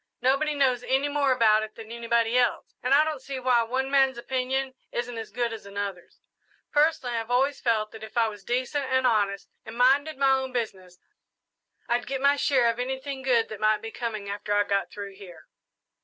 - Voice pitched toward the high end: Yes, high, 245 Hz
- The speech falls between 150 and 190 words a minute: No, fast, 205 wpm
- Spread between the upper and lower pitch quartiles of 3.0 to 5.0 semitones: Yes, average, 3.5 semitones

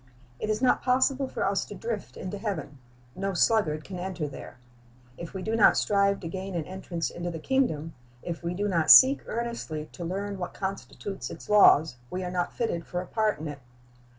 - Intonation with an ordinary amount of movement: Yes, average, 4.0 semitones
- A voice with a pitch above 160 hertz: Yes, high, 190 Hz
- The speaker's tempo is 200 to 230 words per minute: Yes, fast, 205 wpm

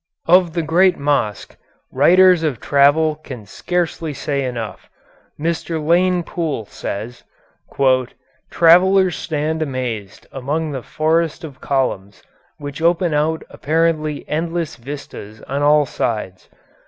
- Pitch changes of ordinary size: Yes, average, 3.9 semitones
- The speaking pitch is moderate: Yes, medium, 150 Hz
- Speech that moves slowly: Yes, slow, 115 wpm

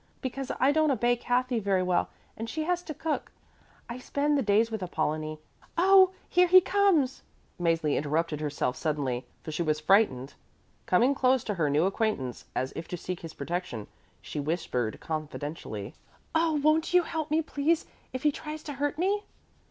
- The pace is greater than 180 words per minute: No, average, 175 wpm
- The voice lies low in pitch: No, high, 225 Hz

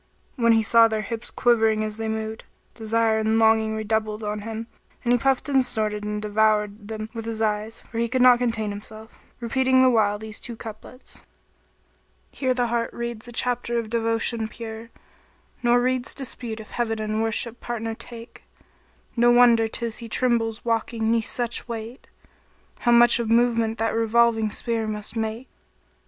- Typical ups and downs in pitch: No, narrow, 1.4 semitones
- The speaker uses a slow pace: No, average, 175 wpm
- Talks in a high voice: Yes, high, 225 Hz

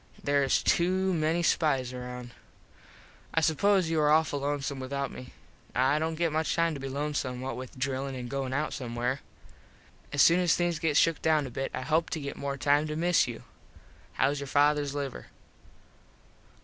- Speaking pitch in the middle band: Yes, medium, 145 Hz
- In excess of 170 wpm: Yes, average, 185 wpm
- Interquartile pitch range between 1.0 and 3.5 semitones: Yes, average, 3.1 semitones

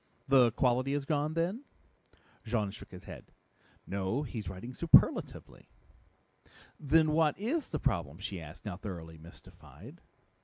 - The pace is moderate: No, slow, 130 wpm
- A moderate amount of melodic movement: No, wide, 8.2 semitones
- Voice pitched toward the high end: No, low, 125 Hz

